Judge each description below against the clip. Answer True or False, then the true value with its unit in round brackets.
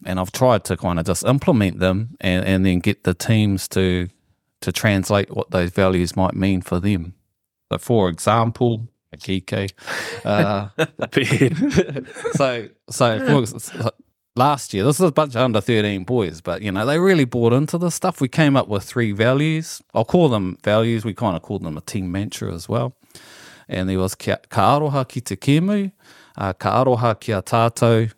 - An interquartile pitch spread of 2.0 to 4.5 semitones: False (5.1 semitones)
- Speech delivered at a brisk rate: False (165 wpm)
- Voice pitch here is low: True (105 Hz)